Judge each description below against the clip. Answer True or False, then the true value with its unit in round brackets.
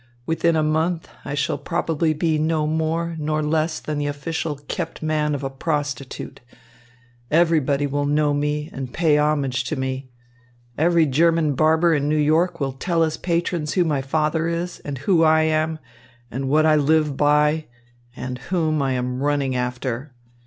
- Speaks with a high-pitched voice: False (150 Hz)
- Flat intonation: True (2.1 semitones)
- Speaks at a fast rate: False (165 wpm)